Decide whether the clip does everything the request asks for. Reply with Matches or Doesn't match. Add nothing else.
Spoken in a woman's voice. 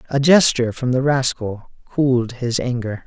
Doesn't match